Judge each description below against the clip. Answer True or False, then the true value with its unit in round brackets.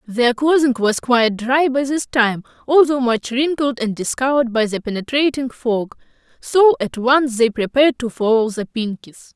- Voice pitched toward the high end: True (250 Hz)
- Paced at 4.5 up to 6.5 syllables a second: True (4.8 syllables/s)